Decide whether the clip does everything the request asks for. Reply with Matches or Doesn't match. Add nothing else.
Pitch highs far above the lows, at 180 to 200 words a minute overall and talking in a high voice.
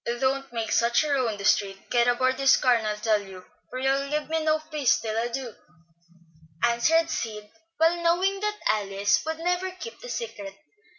Matches